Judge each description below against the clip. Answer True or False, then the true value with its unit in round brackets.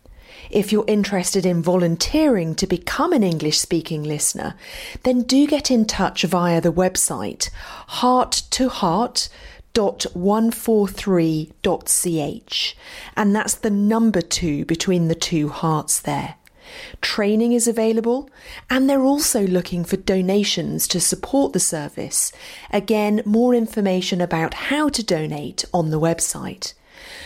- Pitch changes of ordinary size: False (5.9 semitones)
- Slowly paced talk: True (120 wpm)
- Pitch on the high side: True (205 Hz)